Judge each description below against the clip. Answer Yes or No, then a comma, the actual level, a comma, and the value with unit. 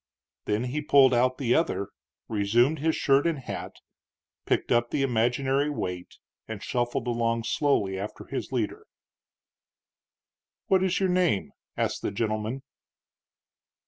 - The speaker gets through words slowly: Yes, slow, 130 wpm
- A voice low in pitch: Yes, low, 125 Hz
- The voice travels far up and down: No, average, 4.3 semitones